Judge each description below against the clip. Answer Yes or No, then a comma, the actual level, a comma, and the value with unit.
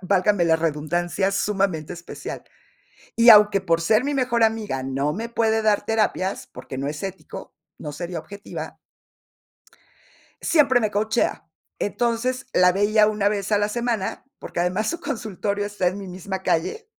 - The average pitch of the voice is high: Yes, high, 205 Hz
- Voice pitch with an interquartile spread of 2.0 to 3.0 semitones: No, average, 3.8 semitones